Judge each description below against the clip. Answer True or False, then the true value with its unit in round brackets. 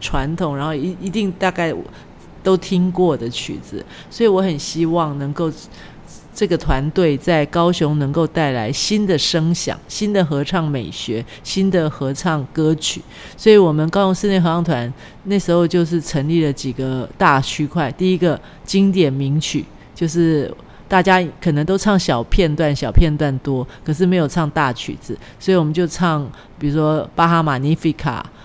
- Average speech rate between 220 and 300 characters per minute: True (250 characters per minute)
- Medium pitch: True (160 Hz)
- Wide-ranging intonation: False (3.9 semitones)